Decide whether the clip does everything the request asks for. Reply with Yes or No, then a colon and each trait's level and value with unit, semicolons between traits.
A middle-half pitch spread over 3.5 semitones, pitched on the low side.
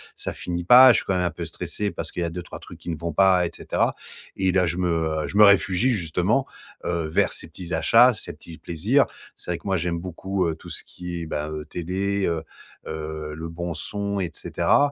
No: average, 2.9 semitones; very low, 90 Hz